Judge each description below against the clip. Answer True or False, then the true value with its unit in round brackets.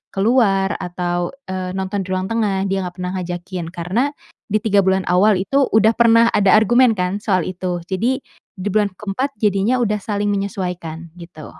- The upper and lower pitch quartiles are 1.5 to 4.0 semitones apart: True (2.8 semitones)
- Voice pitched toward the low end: False (195 Hz)